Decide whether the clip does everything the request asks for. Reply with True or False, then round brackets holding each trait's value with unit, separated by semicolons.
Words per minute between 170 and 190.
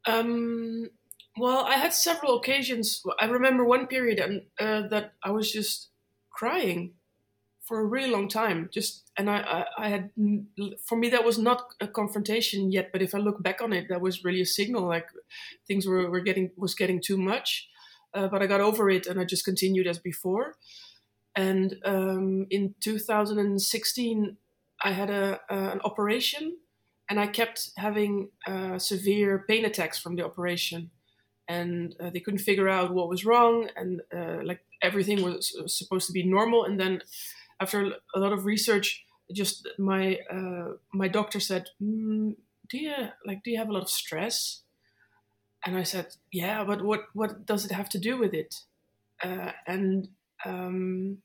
True (180 wpm)